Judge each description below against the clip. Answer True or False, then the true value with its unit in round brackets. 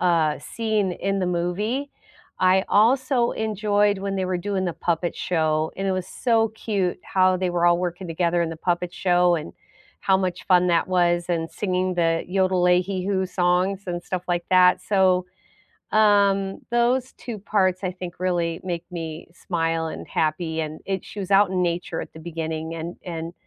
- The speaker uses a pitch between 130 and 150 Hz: False (180 Hz)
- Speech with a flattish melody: True (2.2 semitones)